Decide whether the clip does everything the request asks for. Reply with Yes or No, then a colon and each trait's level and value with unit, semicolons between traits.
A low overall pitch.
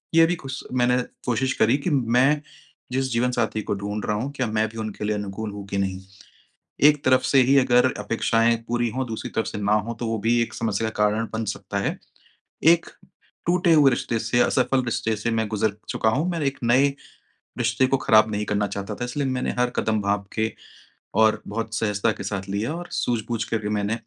Yes: low, 115 Hz